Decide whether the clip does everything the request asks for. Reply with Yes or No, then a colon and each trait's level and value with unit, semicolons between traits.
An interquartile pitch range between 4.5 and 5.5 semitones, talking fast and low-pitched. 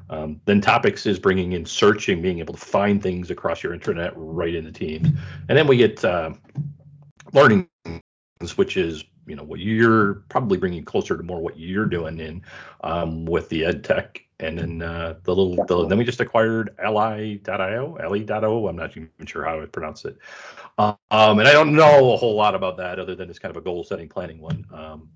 Yes: average, 5.2 semitones; fast, 210 wpm; low, 100 Hz